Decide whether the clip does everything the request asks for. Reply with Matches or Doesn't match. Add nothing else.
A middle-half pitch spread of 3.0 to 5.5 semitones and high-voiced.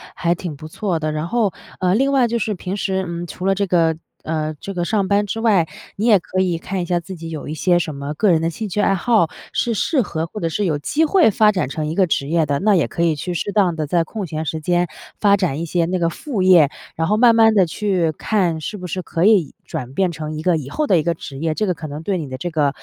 Doesn't match